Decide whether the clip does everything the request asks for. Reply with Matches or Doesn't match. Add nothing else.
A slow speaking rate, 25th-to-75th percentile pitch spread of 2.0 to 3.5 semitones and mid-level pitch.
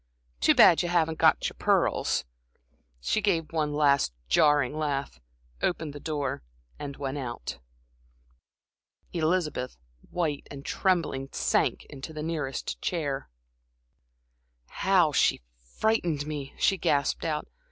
Matches